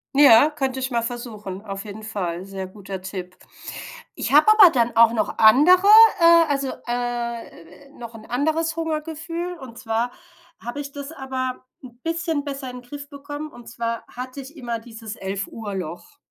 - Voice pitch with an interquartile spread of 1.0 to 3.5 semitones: No, average, 4.6 semitones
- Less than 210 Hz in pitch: No, high, 245 Hz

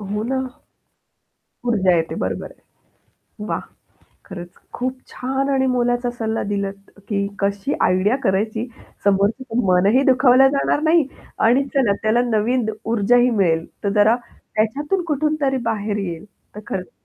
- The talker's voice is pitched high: Yes, high, 220 Hz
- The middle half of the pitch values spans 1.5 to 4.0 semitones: No, average, 4.4 semitones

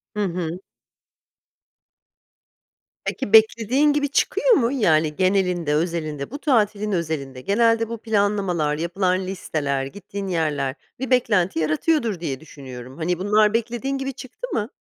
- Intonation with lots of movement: Yes, wide, 6.3 semitones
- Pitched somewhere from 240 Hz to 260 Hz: No, high, 195 Hz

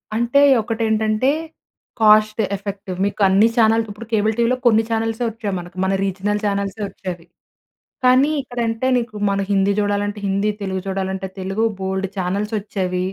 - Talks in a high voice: Yes, high, 205 Hz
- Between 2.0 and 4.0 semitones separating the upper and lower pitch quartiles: Yes, narrow, 2.6 semitones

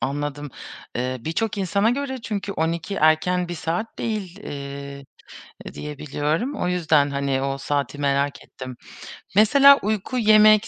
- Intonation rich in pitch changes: Yes, wide, 7.0 semitones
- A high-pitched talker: No, medium, 160 Hz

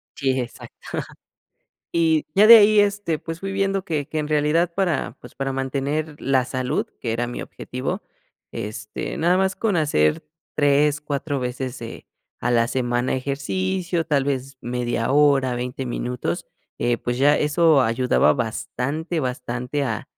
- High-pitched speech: No, medium, 140 Hz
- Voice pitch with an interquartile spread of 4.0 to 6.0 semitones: Yes, average, 4.4 semitones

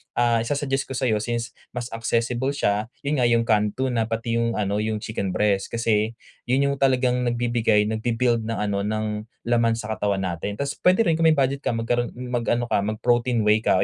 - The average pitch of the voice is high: No, low, 115 Hz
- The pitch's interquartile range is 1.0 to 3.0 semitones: Yes, narrow, 2.4 semitones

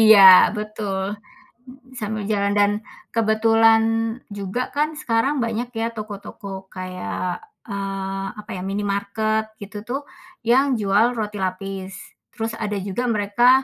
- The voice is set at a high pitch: Yes, high, 210 Hz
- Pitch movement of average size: No, narrow, 2.1 semitones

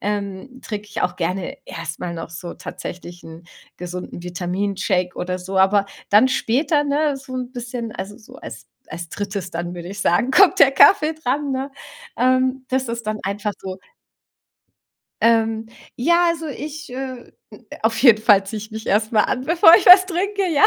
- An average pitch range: No, wide, 6.0 semitones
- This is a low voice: No, high, 220 Hz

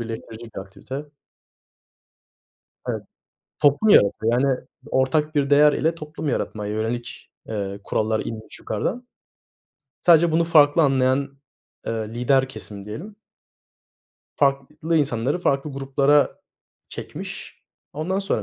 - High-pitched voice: No, low, 135 Hz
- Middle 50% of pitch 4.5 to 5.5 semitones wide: Yes, average, 5.0 semitones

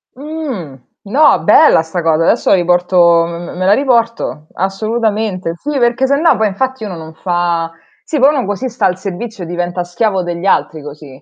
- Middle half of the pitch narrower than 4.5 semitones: No, wide, 5.7 semitones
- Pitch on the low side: No, high, 190 Hz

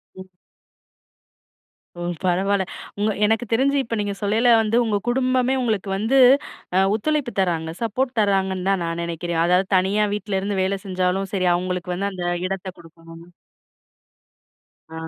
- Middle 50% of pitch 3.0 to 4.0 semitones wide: Yes, average, 3.3 semitones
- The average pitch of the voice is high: Yes, high, 195 Hz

